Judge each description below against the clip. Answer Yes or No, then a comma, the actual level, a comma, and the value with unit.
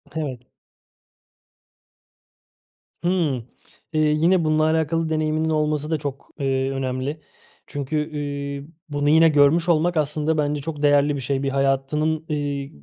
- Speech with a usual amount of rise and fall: No, narrow, 1.9 semitones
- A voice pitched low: No, medium, 150 Hz